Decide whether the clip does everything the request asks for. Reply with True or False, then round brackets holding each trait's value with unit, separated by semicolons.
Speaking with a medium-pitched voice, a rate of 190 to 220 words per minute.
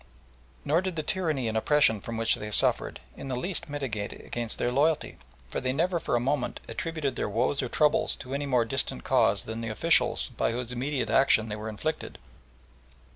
False (130 Hz; 195 wpm)